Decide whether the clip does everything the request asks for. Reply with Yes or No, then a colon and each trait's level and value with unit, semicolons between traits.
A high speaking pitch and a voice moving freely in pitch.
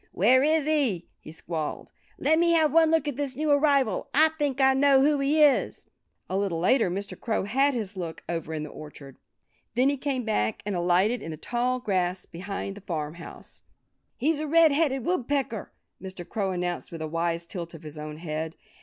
Yes: high, 220 Hz; wide, 8.7 semitones